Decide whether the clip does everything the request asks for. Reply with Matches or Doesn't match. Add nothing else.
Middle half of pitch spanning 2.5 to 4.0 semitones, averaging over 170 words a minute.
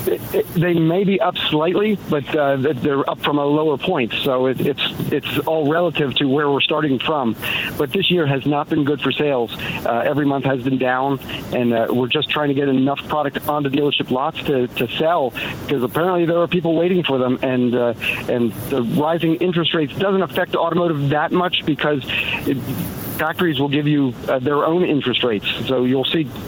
Matches